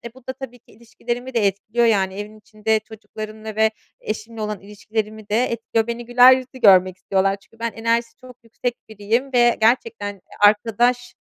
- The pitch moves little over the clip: Yes, narrow, 2.3 semitones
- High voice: Yes, high, 225 Hz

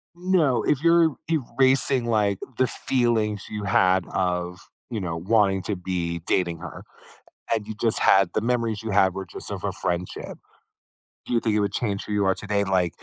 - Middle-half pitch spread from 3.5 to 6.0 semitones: Yes, average, 4.0 semitones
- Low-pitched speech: Yes, low, 105 Hz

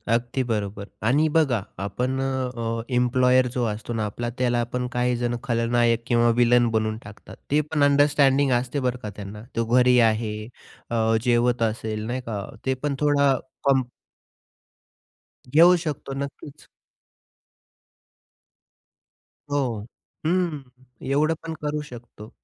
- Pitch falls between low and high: No, low, 125 Hz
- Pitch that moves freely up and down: No, average, 3.3 semitones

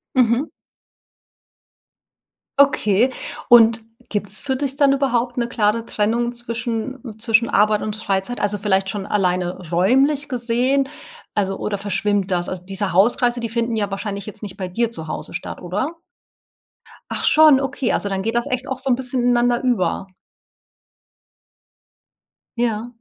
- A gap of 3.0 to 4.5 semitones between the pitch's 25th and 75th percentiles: Yes, average, 3.5 semitones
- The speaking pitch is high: Yes, high, 230 Hz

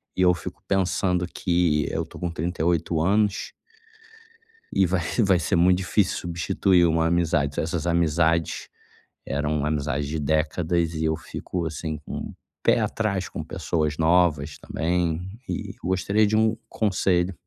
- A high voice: No, very low, 85 Hz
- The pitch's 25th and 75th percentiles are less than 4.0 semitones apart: Yes, narrow, 2.6 semitones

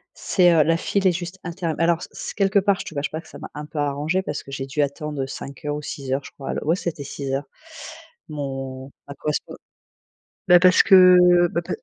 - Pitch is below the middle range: No, medium, 155 Hz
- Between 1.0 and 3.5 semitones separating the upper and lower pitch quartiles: No, average, 4.0 semitones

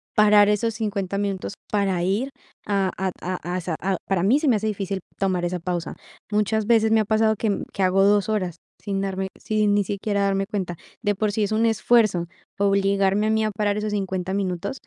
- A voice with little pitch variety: Yes, narrow, 2.0 semitones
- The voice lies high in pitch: Yes, high, 200 Hz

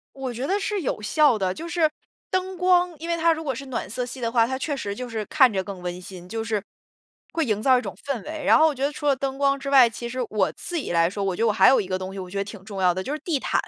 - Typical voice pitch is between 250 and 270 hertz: Yes, very high, 255 Hz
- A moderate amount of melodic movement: No, wide, 6.8 semitones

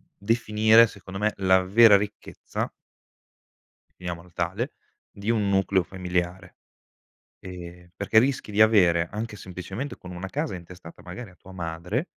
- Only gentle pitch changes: No, average, 3.3 semitones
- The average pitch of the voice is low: Yes, very low, 95 Hz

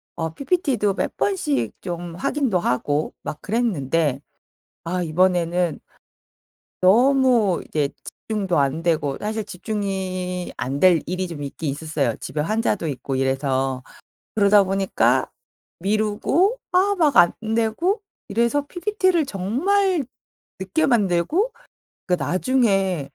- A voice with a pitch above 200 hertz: No, high, 190 Hz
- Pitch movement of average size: No, wide, 6.9 semitones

